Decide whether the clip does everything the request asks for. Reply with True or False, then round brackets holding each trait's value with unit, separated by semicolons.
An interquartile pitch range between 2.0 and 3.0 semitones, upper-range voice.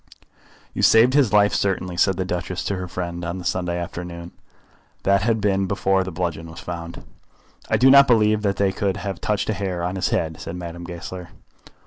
False (2.5 semitones; 95 Hz)